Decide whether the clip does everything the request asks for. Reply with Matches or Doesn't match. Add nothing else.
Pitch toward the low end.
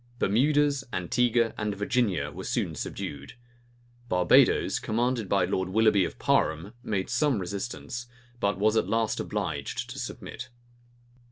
Matches